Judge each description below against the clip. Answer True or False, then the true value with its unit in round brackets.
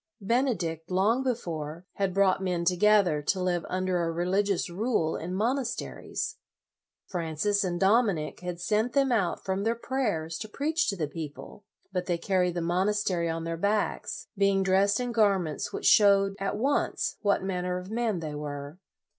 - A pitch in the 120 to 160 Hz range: False (190 Hz)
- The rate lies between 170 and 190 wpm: True (180 wpm)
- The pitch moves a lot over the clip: False (3.5 semitones)